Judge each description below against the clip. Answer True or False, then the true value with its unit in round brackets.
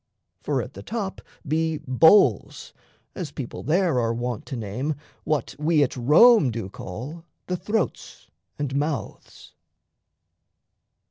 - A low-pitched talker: False (150 Hz)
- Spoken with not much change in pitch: False (5.3 semitones)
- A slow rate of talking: True (125 wpm)